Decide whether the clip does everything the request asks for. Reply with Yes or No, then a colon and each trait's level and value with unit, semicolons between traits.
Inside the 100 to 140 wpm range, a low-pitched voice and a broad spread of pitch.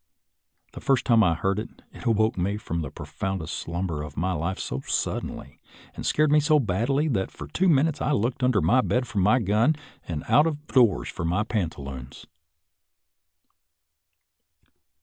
No: average, 170 wpm; low, 105 Hz; wide, 7.4 semitones